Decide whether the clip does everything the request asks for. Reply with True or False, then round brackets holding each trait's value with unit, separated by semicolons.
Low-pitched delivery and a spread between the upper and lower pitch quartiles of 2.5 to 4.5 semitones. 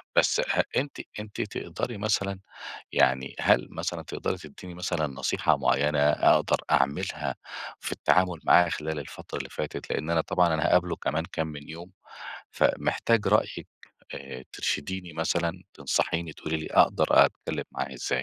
True (80 Hz; 3.3 semitones)